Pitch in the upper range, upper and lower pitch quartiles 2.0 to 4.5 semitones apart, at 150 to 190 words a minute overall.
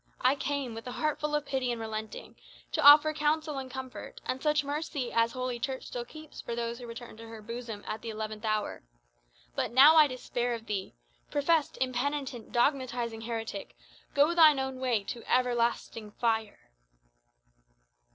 Yes: very high, 250 Hz; average, 3.8 semitones; average, 170 wpm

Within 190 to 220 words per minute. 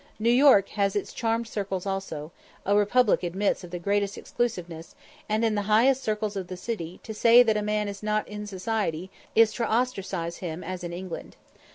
Yes: average, 195 wpm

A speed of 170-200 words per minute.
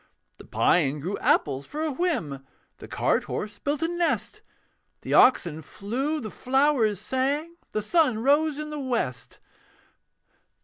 No: average, 140 wpm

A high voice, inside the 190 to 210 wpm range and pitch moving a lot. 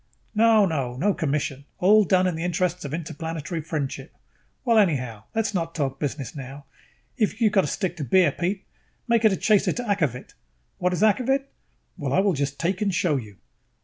No: medium, 175 Hz; average, 195 wpm; wide, 6.1 semitones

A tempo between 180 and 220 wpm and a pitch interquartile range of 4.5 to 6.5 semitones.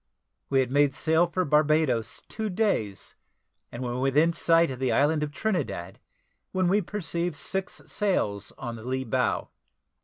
No: average, 155 wpm; average, 5.3 semitones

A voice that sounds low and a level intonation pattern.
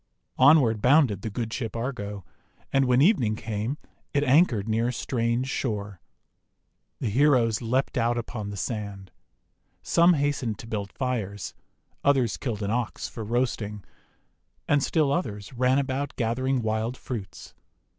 No: low, 120 Hz; average, 3.8 semitones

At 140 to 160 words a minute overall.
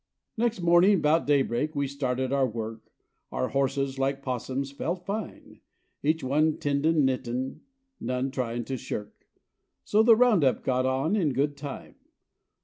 Yes: average, 150 wpm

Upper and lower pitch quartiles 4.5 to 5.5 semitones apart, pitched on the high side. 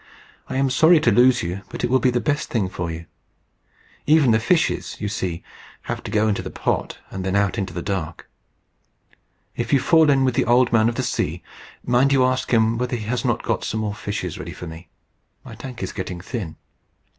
No: average, 5.1 semitones; low, 115 Hz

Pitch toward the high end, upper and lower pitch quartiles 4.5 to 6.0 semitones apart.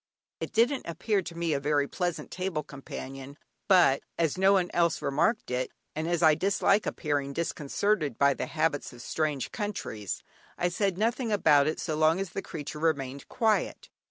No: medium, 160 Hz; average, 5.1 semitones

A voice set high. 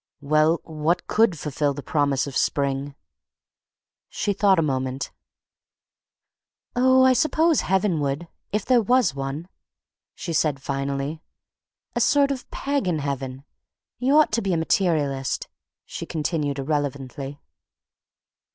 No: medium, 155 Hz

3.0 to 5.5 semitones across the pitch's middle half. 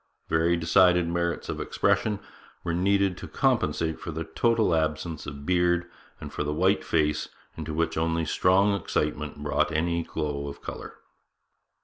No: narrow, 2.6 semitones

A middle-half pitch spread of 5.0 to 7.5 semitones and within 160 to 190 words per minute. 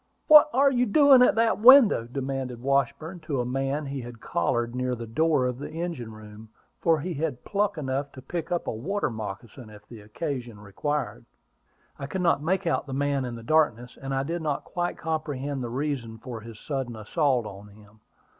No: wide, 5.4 semitones; average, 200 wpm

